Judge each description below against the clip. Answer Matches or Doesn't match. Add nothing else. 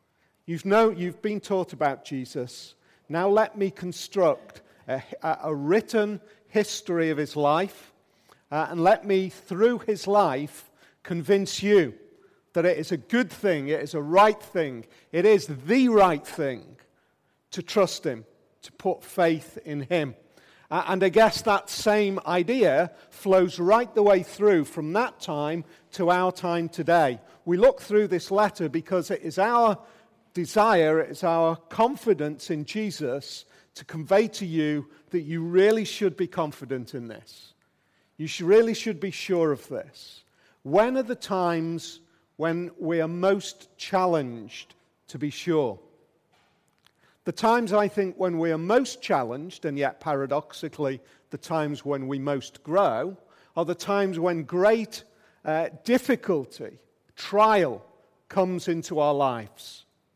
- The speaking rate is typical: Matches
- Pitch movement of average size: Matches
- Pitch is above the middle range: Doesn't match